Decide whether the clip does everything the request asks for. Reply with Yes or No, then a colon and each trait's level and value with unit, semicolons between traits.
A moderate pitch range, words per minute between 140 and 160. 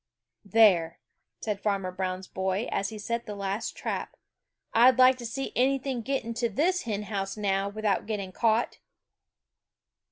Yes: average, 3.3 semitones; average, 150 wpm